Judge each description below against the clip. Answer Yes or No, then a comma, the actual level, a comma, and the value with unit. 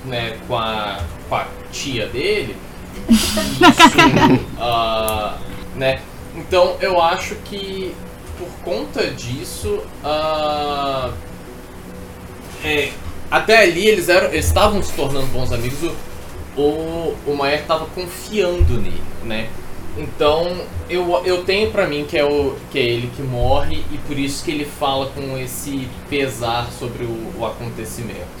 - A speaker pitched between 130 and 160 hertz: Yes, medium, 140 Hz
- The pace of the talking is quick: No, average, 130 wpm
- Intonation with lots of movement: Yes, wide, 6.7 semitones